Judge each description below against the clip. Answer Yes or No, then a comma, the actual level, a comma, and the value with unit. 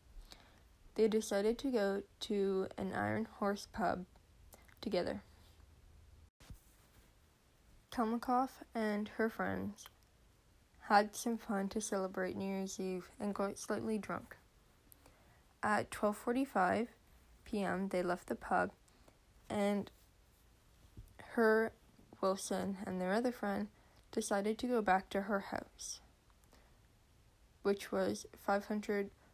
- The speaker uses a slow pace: Yes, slow, 100 wpm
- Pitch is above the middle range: Yes, high, 200 Hz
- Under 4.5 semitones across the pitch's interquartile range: Yes, average, 3.1 semitones